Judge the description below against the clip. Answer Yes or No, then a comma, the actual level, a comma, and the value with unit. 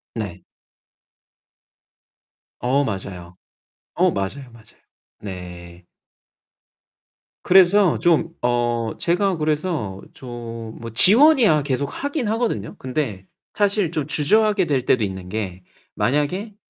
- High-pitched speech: No, low, 135 Hz